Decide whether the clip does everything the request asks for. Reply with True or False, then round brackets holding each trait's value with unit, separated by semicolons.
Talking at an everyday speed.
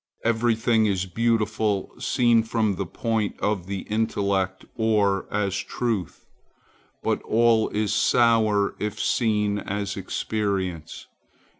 False (115 wpm)